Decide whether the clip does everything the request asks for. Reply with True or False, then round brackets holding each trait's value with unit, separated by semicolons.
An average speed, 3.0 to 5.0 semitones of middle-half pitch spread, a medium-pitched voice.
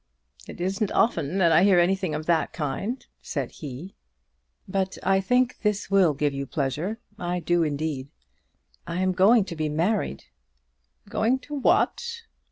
True (160 wpm; 4.2 semitones; 180 Hz)